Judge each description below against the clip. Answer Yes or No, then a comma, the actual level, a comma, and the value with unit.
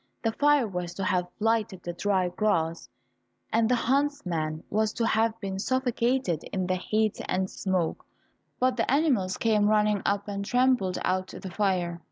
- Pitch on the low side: No, high, 205 Hz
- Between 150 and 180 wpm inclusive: Yes, average, 165 wpm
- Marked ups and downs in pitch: No, average, 3.8 semitones